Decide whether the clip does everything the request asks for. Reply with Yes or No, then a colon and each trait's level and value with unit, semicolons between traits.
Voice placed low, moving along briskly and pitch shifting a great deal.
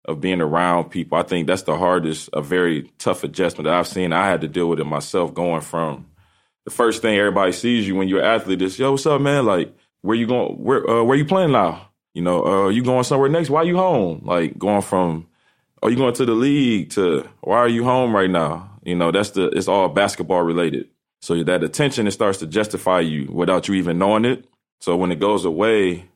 Yes: very low, 95 Hz; fast, 240 wpm; wide, 5.8 semitones